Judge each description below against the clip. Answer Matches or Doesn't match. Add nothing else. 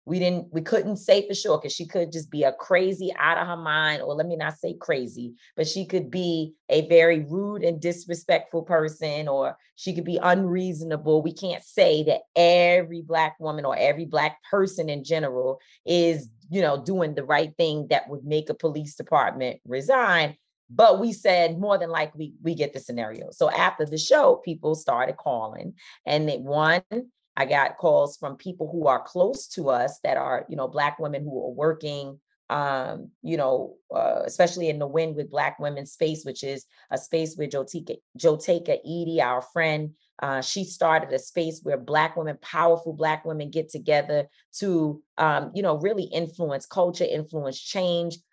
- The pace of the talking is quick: Doesn't match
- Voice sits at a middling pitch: Matches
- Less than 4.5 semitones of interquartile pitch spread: Matches